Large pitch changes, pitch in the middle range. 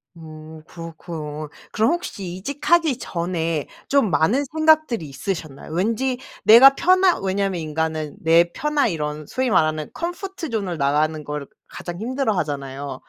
Yes: wide, 8.8 semitones; medium, 175 Hz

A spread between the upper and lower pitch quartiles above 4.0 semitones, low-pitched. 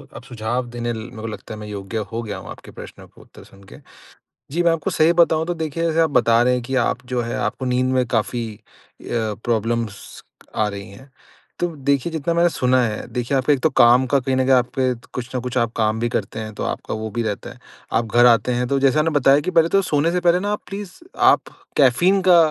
Yes: average, 4.7 semitones; low, 125 Hz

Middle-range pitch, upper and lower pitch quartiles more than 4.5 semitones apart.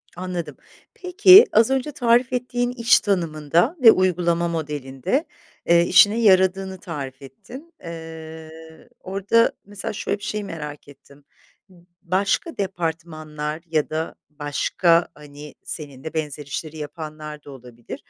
Yes: medium, 170 Hz; average, 5.0 semitones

